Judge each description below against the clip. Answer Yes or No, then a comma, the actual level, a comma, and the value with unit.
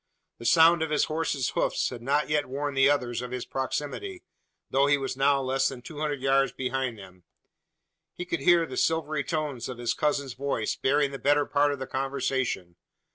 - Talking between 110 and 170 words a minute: No, average, 195 wpm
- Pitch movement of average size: No, narrow, 2.3 semitones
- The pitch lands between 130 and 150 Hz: Yes, medium, 140 Hz